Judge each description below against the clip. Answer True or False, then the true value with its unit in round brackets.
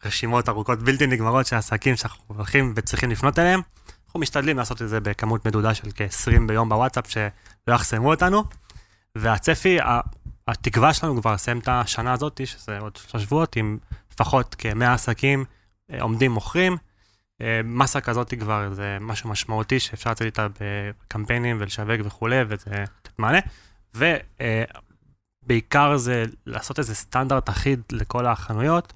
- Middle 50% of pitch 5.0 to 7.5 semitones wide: False (3.7 semitones)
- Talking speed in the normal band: True (135 wpm)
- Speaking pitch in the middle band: False (115 Hz)